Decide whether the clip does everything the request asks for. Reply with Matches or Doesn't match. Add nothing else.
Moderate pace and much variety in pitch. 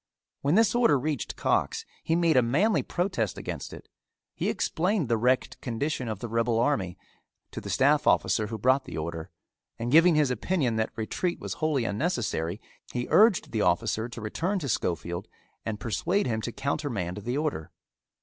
Matches